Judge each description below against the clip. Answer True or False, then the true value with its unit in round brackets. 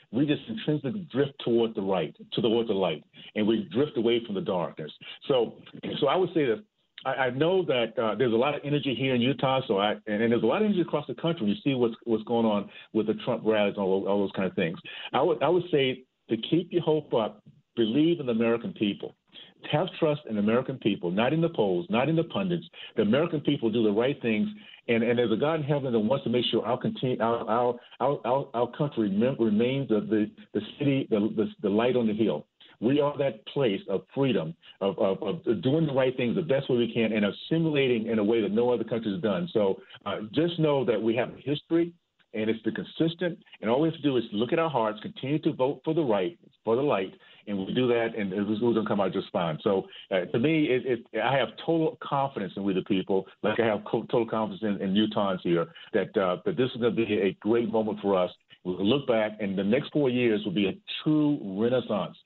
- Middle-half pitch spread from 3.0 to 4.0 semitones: False (5.3 semitones)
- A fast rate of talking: True (250 wpm)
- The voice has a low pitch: True (120 Hz)